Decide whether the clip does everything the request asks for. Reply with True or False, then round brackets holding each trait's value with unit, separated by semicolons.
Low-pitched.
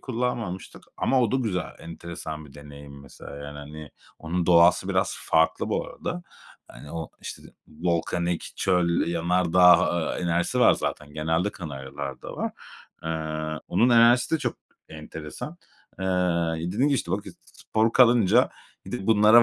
True (85 Hz)